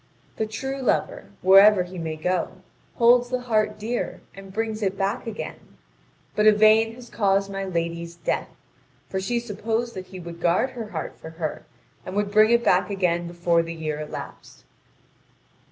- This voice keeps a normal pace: Yes, average, 170 wpm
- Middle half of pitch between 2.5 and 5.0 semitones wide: Yes, average, 4.2 semitones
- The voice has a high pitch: Yes, high, 195 Hz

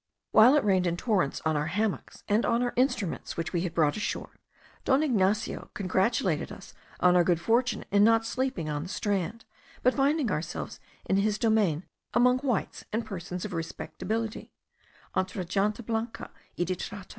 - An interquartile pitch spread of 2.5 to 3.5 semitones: No, average, 4.4 semitones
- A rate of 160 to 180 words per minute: Yes, average, 170 wpm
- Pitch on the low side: No, high, 205 Hz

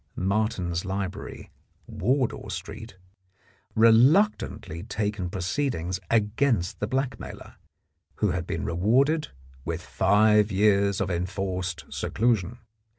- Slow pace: Yes, slow, 90 wpm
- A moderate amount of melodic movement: Yes, average, 3.8 semitones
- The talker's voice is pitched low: Yes, low, 105 Hz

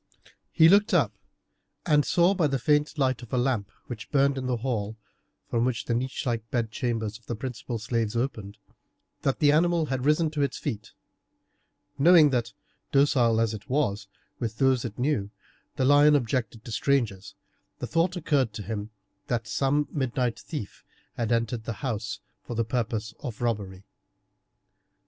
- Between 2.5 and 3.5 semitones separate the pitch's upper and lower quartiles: No, average, 4.1 semitones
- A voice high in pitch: No, low, 125 Hz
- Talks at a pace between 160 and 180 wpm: Yes, average, 170 wpm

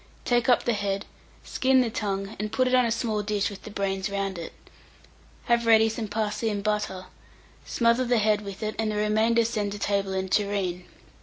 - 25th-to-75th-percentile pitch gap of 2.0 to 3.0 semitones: Yes, narrow, 2.5 semitones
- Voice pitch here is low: No, high, 210 Hz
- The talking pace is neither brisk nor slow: No, fast, 210 wpm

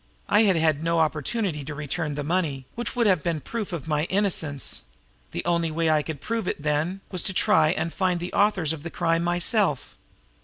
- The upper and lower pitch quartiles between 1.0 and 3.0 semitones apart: No, average, 3.6 semitones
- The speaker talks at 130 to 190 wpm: No, fast, 205 wpm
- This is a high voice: No, medium, 165 Hz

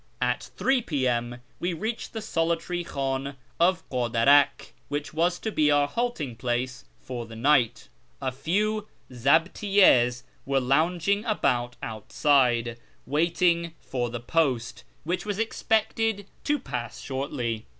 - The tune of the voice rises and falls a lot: Yes, wide, 6.4 semitones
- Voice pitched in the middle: Yes, medium, 145 Hz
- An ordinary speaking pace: No, slow, 125 wpm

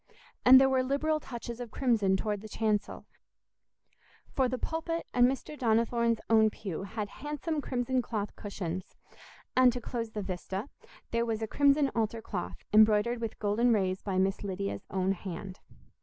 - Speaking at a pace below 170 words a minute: Yes, average, 160 wpm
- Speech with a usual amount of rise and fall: Yes, average, 3.9 semitones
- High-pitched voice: Yes, high, 225 Hz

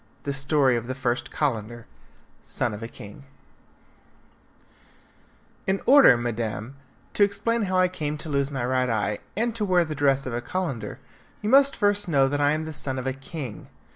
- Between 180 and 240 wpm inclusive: Yes, average, 185 wpm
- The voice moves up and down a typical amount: No, wide, 7.1 semitones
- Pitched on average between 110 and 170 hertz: Yes, medium, 140 Hz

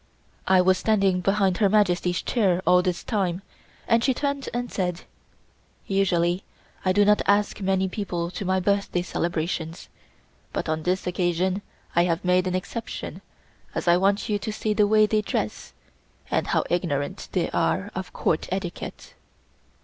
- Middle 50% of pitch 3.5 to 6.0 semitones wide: No, narrow, 2.5 semitones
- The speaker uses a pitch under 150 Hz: No, medium, 185 Hz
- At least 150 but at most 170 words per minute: Yes, average, 160 wpm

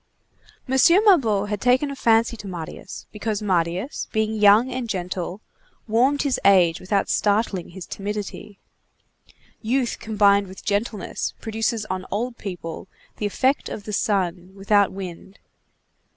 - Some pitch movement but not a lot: Yes, average, 3.1 semitones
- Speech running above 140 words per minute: No, slow, 135 wpm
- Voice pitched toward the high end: Yes, high, 205 Hz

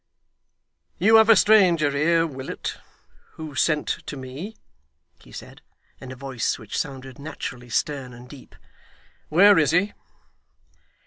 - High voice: No, medium, 145 Hz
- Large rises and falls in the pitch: No, average, 4.5 semitones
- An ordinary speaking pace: No, slow, 130 wpm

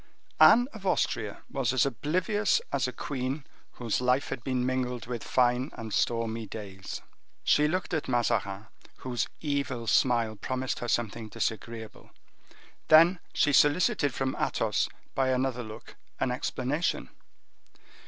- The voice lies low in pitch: Yes, low, 125 Hz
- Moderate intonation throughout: Yes, average, 3.4 semitones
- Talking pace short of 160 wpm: Yes, slow, 135 wpm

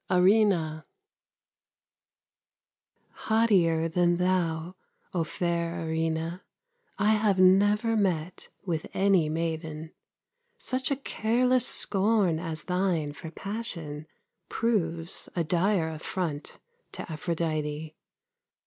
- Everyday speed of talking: No, slow, 90 wpm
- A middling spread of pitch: Yes, average, 3.7 semitones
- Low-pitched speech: No, medium, 175 Hz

